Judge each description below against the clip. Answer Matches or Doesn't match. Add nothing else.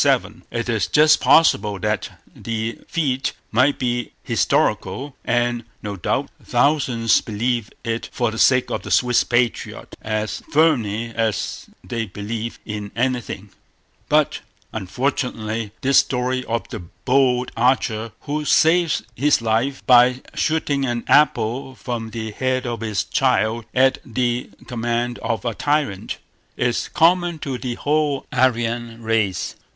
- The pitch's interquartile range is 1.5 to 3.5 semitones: Matches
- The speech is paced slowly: Matches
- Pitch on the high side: Doesn't match